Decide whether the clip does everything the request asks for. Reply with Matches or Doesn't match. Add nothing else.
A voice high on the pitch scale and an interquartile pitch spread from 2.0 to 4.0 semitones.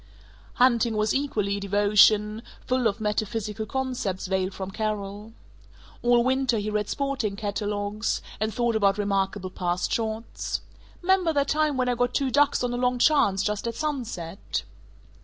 Matches